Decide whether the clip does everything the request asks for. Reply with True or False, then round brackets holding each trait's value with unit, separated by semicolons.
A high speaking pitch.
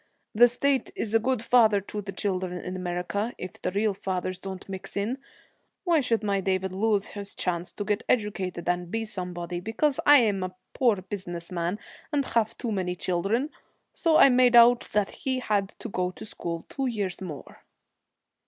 True (200 Hz)